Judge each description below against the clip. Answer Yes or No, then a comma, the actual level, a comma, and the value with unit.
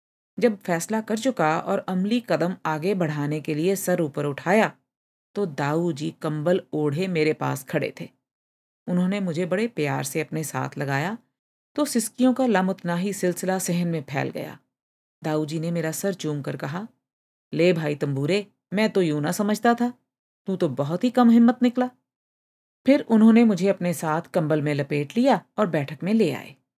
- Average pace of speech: No, fast, 180 wpm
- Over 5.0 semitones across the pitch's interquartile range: Yes, wide, 5.5 semitones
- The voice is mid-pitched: Yes, medium, 180 Hz